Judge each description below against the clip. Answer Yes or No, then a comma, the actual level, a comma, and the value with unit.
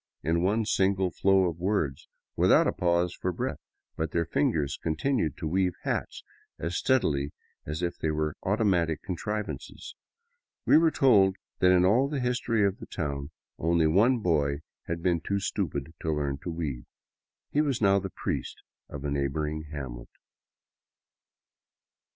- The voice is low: Yes, very low, 85 Hz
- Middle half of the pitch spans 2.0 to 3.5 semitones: No, average, 4.4 semitones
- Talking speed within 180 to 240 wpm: No, average, 155 wpm